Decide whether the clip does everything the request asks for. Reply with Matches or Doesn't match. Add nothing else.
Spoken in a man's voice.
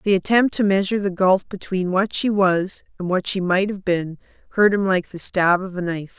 Doesn't match